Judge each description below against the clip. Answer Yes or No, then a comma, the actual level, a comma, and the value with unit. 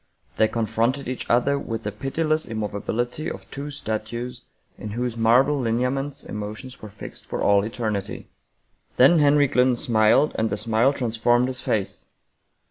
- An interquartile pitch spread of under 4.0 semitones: Yes, average, 3.6 semitones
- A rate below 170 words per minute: Yes, average, 150 wpm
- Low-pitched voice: Yes, low, 120 Hz